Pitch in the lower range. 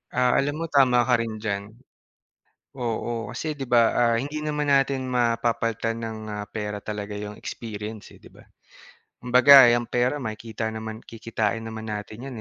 Yes: low, 115 Hz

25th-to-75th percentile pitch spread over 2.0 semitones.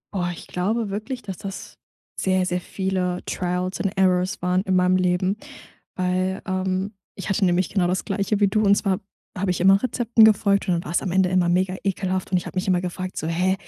No: narrow, 1.5 semitones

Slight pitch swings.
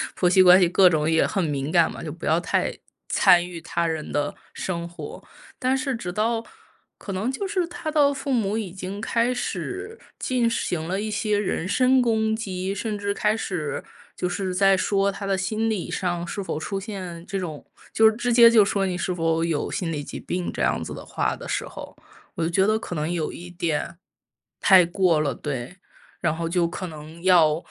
No: average, 4.4 semitones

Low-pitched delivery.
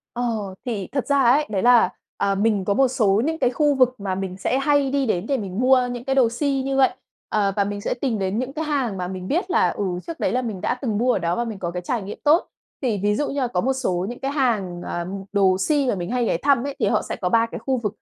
No: high, 235 Hz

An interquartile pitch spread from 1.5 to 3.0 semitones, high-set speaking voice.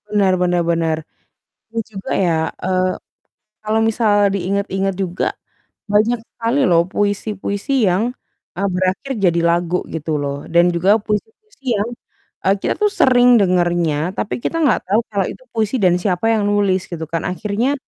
No: average, 3.7 semitones; high, 195 Hz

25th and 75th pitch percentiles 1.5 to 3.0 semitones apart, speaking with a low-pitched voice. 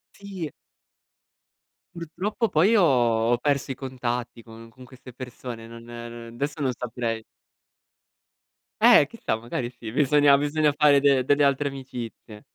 No: average, 3.6 semitones; low, 130 Hz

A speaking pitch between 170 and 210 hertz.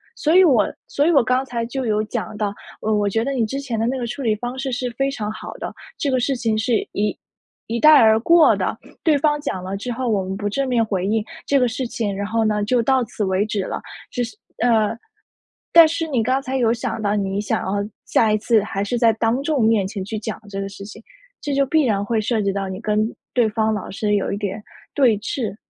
No: high, 225 Hz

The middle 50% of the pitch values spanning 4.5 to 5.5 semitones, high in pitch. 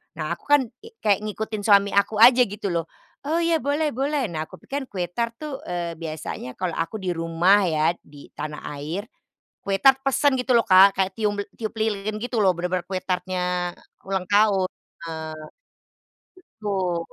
Yes: average, 4.8 semitones; high, 195 Hz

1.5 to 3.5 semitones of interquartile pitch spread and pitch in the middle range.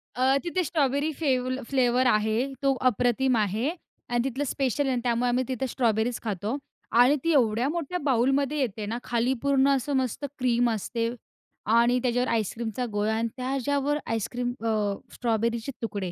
No: average, 2.8 semitones; high, 245 Hz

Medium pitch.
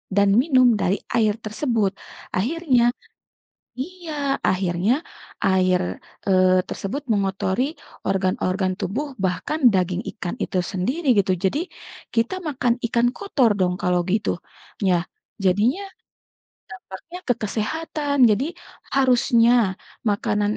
No: high, 210 Hz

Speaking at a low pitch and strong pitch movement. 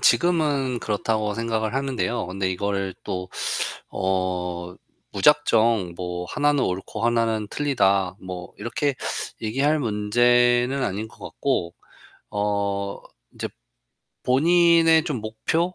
Yes: low, 110 Hz; wide, 5.7 semitones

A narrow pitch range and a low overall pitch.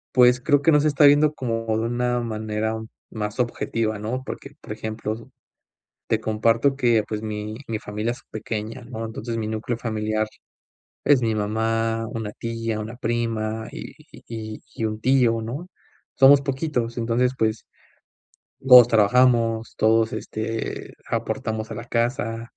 Yes: narrow, 2.0 semitones; low, 115 Hz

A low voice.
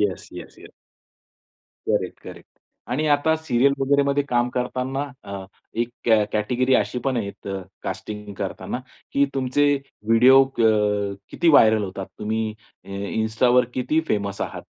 Yes: low, 120 Hz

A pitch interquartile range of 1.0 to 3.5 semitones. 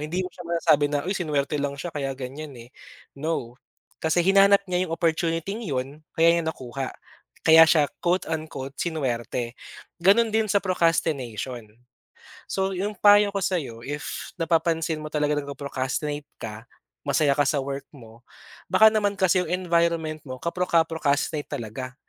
No: average, 4.0 semitones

